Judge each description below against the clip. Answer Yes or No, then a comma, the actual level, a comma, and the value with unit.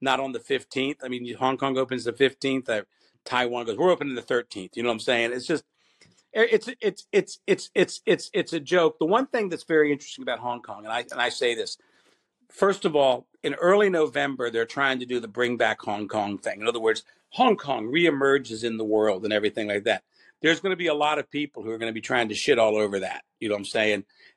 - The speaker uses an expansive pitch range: Yes, wide, 5.7 semitones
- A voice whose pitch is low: Yes, low, 130 Hz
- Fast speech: Yes, fast, 250 wpm